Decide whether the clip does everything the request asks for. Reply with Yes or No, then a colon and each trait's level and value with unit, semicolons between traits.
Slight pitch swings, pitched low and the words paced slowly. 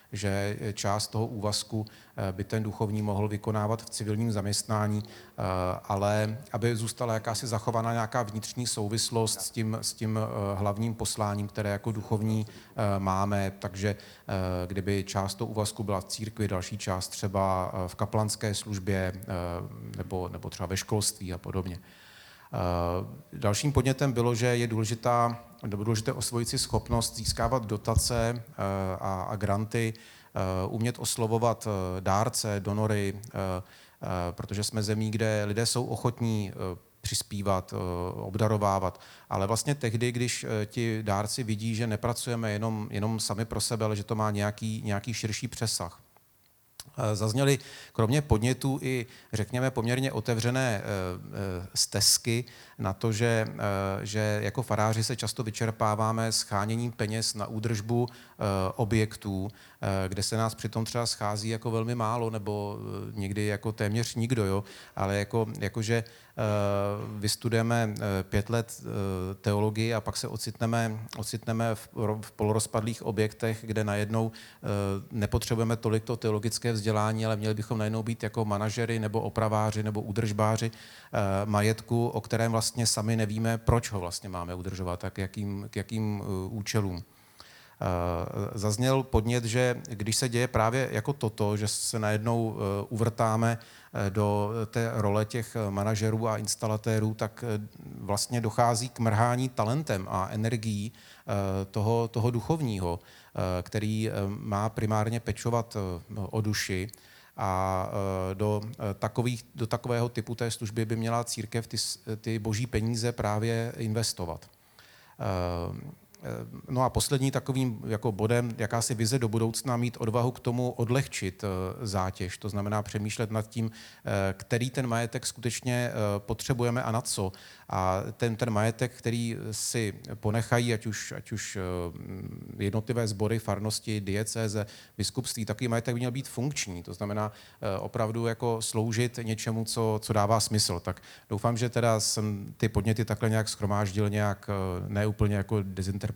No: narrow, 2.2 semitones; low, 110 Hz; average, 130 wpm